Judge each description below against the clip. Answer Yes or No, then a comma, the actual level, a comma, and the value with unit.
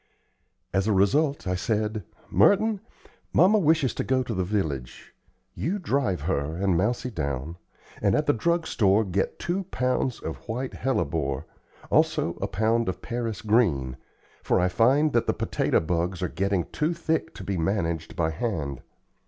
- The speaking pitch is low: Yes, low, 105 Hz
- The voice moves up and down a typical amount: No, wide, 7.1 semitones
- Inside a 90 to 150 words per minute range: No, average, 160 wpm